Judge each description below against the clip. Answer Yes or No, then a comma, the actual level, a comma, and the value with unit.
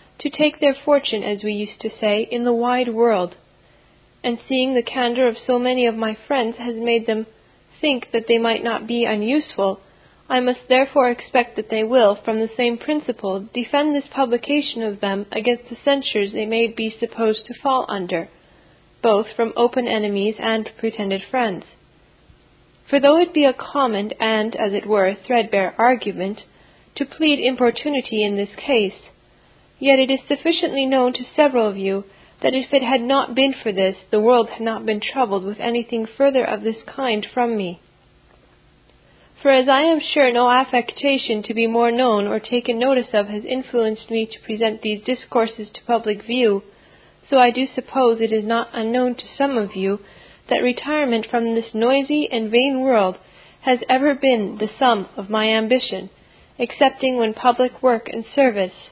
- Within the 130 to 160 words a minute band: No, average, 175 wpm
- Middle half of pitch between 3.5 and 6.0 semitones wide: No, average, 3.1 semitones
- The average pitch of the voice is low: No, high, 235 Hz